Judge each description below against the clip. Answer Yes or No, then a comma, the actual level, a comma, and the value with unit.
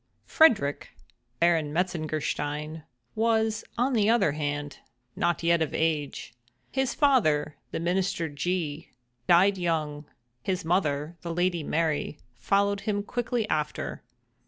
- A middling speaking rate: No, slow, 115 wpm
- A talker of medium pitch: Yes, medium, 170 Hz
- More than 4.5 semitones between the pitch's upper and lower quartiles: Yes, average, 4.9 semitones